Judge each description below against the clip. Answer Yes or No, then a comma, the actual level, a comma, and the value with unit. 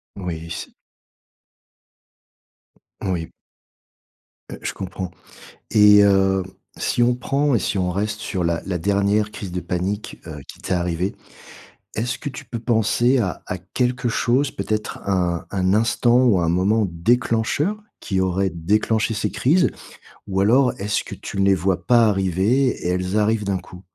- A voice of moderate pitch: No, low, 100 Hz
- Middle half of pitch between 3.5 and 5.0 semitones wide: Yes, average, 3.8 semitones